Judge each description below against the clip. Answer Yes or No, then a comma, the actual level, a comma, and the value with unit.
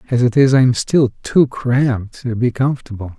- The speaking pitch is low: Yes, low, 120 Hz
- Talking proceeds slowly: No, fast, 205 wpm